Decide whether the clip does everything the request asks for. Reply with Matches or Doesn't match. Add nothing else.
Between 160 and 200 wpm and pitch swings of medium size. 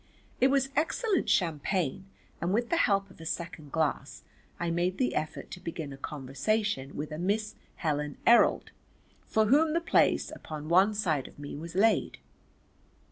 Doesn't match